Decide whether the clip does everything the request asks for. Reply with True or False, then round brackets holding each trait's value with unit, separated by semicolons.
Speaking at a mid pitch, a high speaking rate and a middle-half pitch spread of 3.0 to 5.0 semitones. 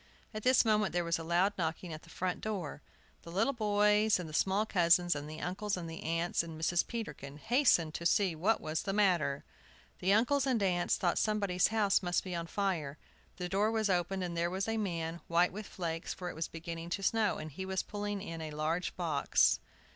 True (180 Hz; 215 wpm; 3.8 semitones)